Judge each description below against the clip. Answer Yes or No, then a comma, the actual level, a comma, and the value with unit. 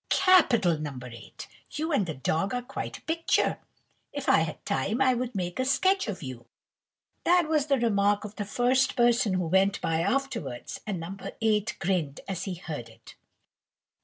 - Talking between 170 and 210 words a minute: Yes, average, 180 wpm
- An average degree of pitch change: No, wide, 7.7 semitones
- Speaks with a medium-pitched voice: No, high, 205 Hz